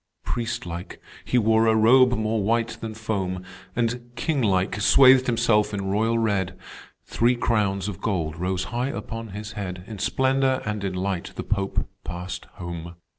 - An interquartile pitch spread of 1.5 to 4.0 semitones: Yes, average, 3.6 semitones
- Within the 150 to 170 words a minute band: Yes, average, 165 wpm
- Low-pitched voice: Yes, low, 110 Hz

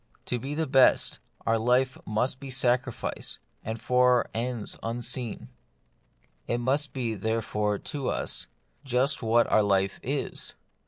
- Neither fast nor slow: No, slow, 130 wpm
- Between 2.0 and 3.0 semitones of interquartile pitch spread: Yes, narrow, 2.6 semitones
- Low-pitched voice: Yes, low, 125 Hz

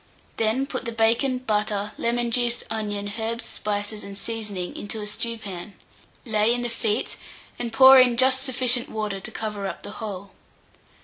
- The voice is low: No, high, 225 Hz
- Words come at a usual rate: Yes, average, 160 wpm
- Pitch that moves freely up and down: No, narrow, 2.5 semitones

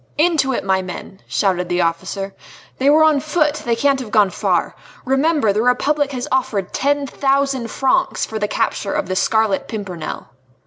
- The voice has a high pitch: Yes, high, 245 Hz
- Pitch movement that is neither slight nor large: No, wide, 6.3 semitones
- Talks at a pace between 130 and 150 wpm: No, average, 175 wpm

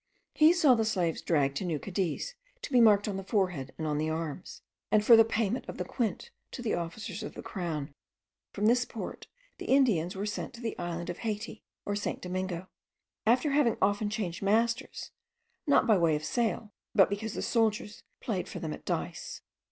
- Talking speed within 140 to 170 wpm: No, average, 200 wpm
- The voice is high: Yes, high, 205 Hz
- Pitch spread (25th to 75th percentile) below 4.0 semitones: No, average, 4.7 semitones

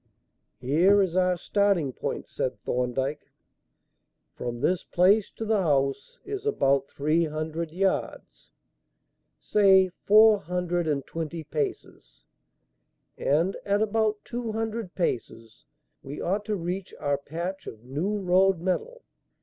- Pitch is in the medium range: Yes, medium, 180 Hz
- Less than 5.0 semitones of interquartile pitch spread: No, wide, 5.5 semitones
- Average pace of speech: No, slow, 125 wpm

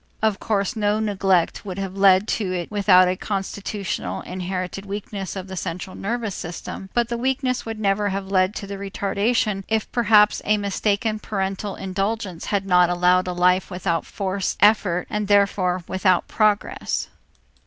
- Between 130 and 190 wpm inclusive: Yes, average, 160 wpm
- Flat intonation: Yes, narrow, 2.2 semitones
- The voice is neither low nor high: No, high, 195 Hz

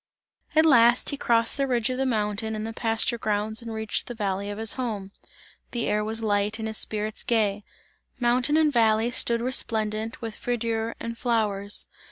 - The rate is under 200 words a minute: Yes, average, 185 wpm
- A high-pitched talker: Yes, high, 225 Hz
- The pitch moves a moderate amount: No, narrow, 2.0 semitones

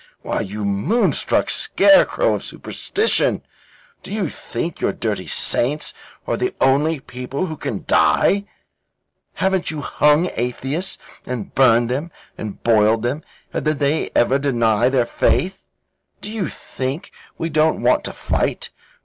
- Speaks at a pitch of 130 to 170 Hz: Yes, medium, 140 Hz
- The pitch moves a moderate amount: No, wide, 6.0 semitones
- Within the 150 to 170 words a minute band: No, average, 140 wpm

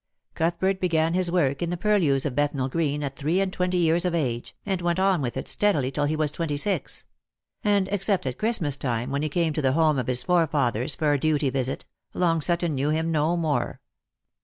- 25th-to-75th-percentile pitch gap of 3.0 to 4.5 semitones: Yes, average, 3.9 semitones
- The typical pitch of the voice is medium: Yes, medium, 155 Hz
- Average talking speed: No, fast, 215 wpm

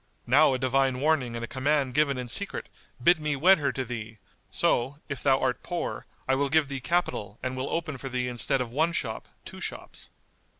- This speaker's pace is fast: Yes, fast, 210 wpm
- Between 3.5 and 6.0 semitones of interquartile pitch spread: No, average, 3.0 semitones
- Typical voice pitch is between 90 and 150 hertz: Yes, low, 135 Hz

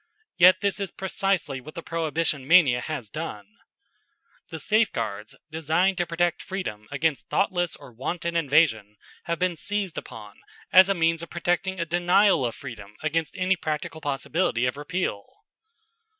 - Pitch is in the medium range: Yes, medium, 165 Hz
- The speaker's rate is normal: Yes, average, 150 wpm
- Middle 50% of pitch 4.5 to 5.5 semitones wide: Yes, average, 5.0 semitones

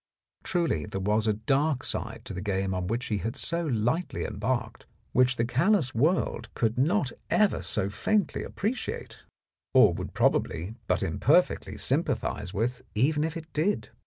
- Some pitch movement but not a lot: No, wide, 7.2 semitones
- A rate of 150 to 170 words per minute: Yes, average, 160 wpm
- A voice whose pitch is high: No, low, 125 Hz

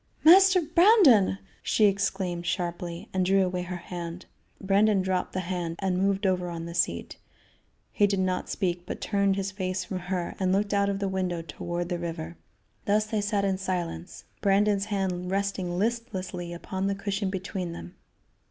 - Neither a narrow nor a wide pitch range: No, narrow, 2.1 semitones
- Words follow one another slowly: No, average, 170 wpm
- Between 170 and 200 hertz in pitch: Yes, high, 190 Hz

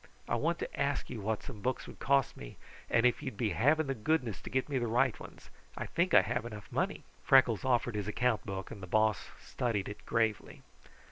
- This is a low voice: Yes, low, 115 Hz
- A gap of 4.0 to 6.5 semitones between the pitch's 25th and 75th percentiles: No, average, 3.5 semitones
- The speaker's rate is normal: No, fast, 220 wpm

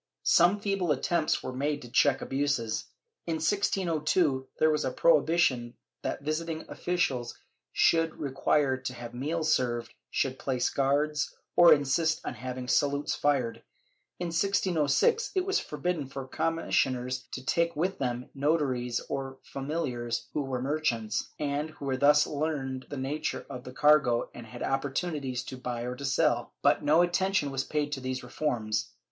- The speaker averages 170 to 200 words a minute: No, average, 155 wpm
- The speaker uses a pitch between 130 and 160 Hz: Yes, medium, 140 Hz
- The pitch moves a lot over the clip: No, average, 3.8 semitones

